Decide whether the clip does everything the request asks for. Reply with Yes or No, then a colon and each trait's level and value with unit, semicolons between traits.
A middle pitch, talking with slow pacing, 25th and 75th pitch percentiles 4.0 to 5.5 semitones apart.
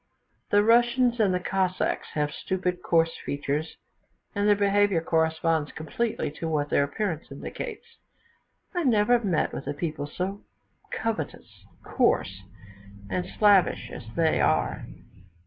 Yes: medium, 180 Hz; slow, 130 wpm; average, 4.7 semitones